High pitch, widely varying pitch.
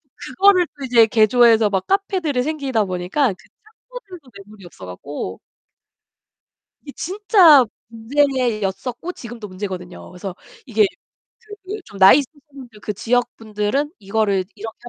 Yes: high, 230 Hz; wide, 6.1 semitones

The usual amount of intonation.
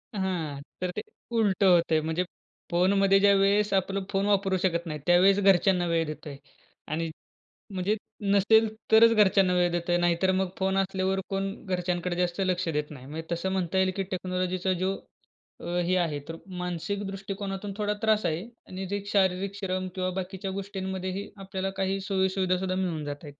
No: narrow, 1.9 semitones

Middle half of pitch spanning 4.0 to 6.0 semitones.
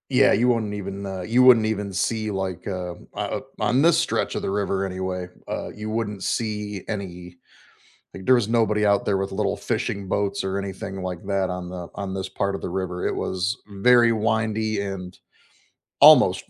No: narrow, 2.4 semitones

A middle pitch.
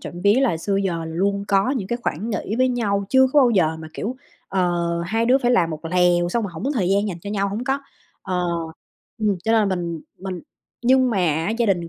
No: high, 200 Hz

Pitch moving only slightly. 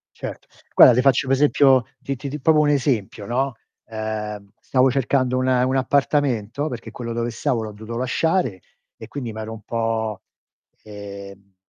No: average, 3.6 semitones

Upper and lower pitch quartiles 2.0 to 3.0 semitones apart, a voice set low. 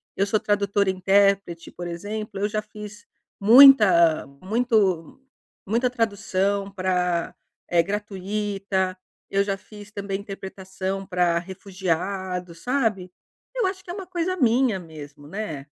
No: narrow, 2.5 semitones; high, 195 Hz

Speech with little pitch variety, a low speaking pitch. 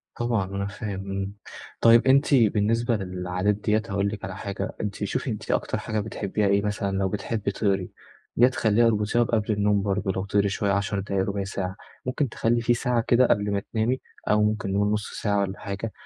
Yes: narrow, 2.3 semitones; low, 105 Hz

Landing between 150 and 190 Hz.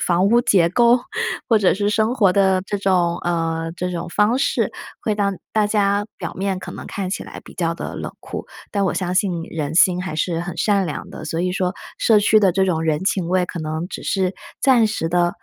Yes: medium, 185 Hz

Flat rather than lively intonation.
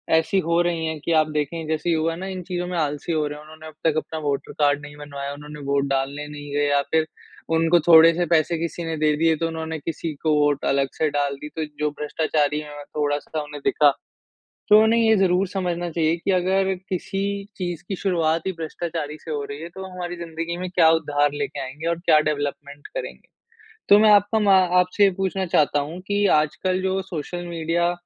No: average, 3.0 semitones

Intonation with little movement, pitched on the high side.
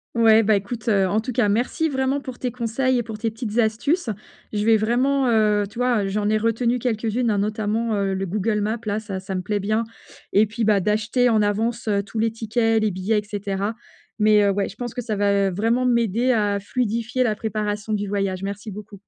Yes: narrow, 2.3 semitones; high, 215 Hz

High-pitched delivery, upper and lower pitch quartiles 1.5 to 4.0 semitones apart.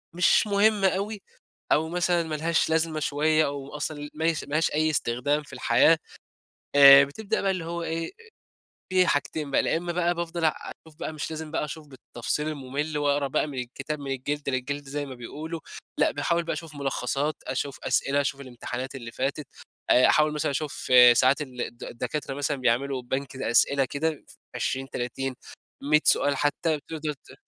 No: medium, 145 Hz; average, 2.8 semitones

